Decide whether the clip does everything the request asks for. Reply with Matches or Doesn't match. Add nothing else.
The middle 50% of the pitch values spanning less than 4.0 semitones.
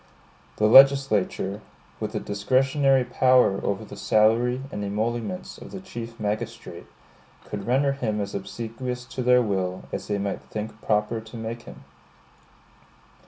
Matches